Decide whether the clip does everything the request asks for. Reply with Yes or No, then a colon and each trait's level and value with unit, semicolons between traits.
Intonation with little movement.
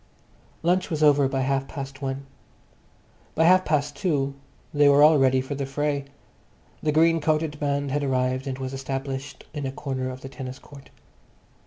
Yes: narrow, 1.9 semitones